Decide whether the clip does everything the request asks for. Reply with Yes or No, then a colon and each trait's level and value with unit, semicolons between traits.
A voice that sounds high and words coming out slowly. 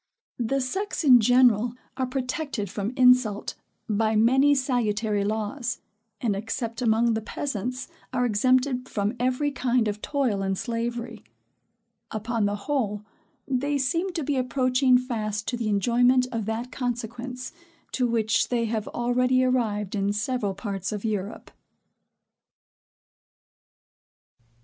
Yes: high, 240 Hz; slow, 125 wpm